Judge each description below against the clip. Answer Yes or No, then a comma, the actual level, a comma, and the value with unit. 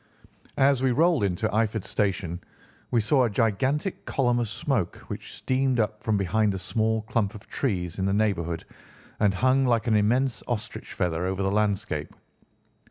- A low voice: Yes, low, 110 Hz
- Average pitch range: Yes, average, 4.1 semitones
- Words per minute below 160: No, average, 165 wpm